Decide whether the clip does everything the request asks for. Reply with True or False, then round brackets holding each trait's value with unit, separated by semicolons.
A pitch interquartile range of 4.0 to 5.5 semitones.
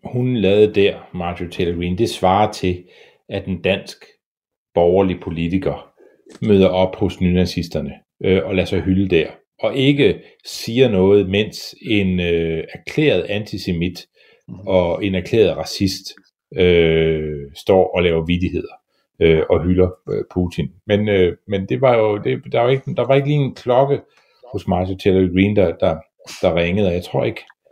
False (2.5 semitones)